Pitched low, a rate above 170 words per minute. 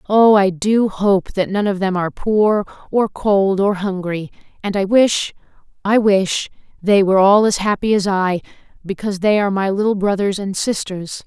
No: high, 200 Hz; average, 180 wpm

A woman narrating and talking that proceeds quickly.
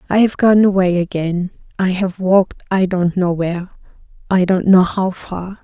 No: female; average, 170 wpm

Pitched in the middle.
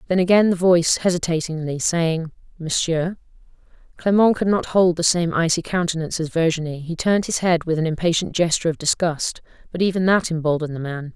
Yes: medium, 170 Hz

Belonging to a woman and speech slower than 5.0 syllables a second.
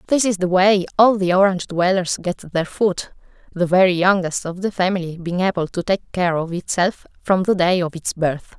No: female; 5.1 syllables/s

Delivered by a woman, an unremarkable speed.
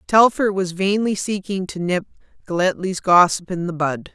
Yes: female; average, 160 wpm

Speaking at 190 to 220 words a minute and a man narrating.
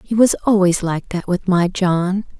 No: average, 200 wpm; female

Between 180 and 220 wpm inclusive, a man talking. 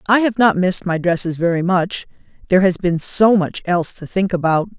No: average, 200 wpm; female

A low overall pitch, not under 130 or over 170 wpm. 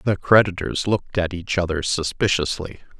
Yes: very low, 90 Hz; average, 140 wpm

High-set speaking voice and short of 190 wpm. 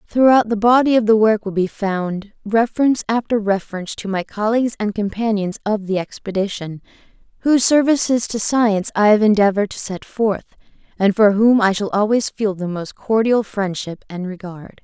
Yes: high, 210 Hz; average, 175 wpm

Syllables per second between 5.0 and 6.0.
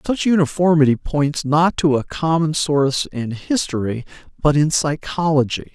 No: 4.6 syllables/s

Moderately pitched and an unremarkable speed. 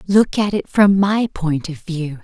No: medium, 180 Hz; fast, 215 wpm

